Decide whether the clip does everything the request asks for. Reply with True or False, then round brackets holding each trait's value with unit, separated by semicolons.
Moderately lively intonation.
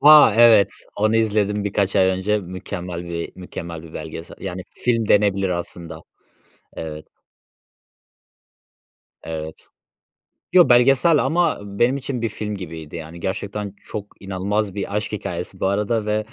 True (3.4 semitones)